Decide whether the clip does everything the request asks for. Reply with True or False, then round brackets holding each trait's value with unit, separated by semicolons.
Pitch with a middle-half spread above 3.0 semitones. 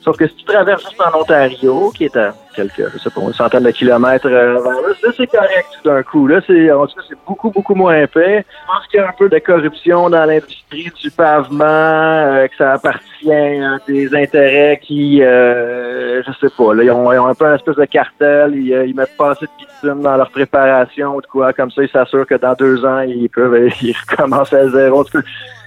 True (3.5 semitones)